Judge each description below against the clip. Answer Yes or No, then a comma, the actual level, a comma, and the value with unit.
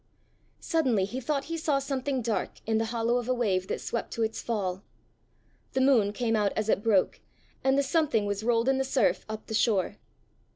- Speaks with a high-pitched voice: Yes, high, 230 Hz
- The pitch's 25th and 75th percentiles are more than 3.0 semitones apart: Yes, average, 3.8 semitones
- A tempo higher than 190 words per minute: Yes, fast, 205 wpm